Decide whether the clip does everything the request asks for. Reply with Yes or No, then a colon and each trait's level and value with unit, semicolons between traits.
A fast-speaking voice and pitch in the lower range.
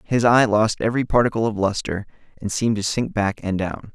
Yes: fast, 215 wpm; low, 110 Hz